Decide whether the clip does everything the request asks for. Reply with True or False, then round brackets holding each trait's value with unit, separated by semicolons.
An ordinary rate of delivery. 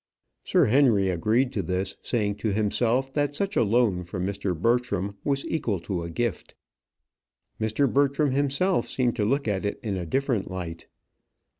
True (165 wpm)